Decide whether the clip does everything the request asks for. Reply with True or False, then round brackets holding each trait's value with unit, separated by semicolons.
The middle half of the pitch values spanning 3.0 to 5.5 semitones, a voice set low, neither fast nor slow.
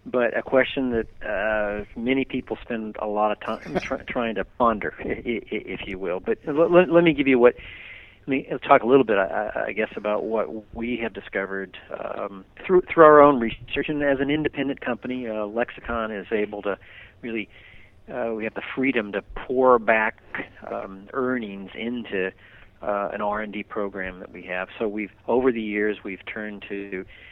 True (3.8 semitones; 110 Hz; 190 wpm)